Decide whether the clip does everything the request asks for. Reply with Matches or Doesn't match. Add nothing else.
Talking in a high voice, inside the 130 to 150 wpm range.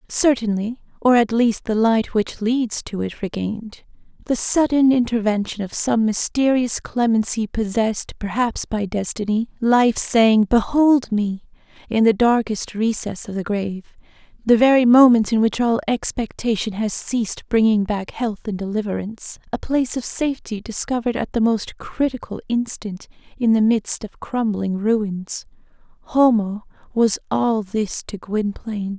Matches